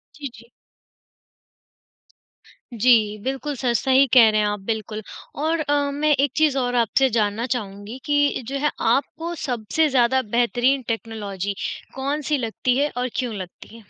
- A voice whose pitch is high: Yes, very high, 250 Hz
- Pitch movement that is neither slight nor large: Yes, average, 4.0 semitones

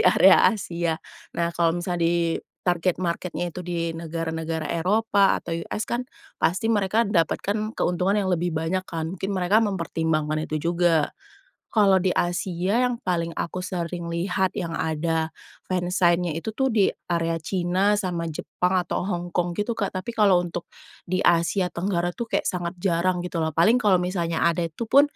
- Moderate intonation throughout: No, narrow, 2.3 semitones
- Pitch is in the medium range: Yes, medium, 175 Hz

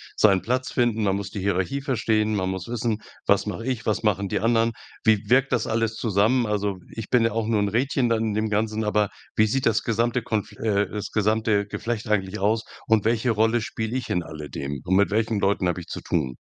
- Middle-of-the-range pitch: No, low, 110 Hz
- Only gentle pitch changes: Yes, narrow, 2.1 semitones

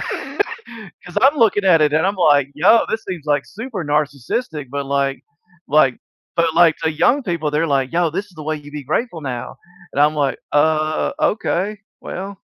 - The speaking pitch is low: No, medium, 155 Hz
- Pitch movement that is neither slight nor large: Yes, average, 4.8 semitones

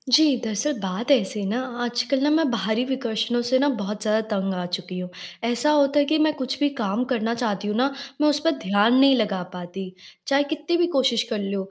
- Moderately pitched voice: No, high, 235 Hz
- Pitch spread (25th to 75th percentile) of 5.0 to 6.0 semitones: Yes, wide, 5.4 semitones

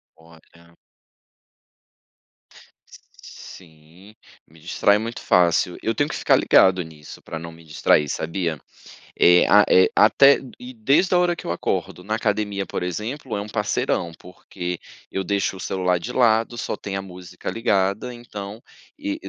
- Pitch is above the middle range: No, very low, 95 Hz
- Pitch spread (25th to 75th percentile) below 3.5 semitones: No, average, 4.2 semitones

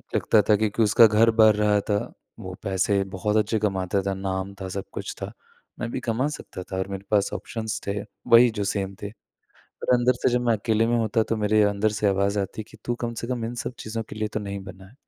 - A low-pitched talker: Yes, low, 105 Hz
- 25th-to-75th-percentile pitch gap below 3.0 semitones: Yes, narrow, 2.4 semitones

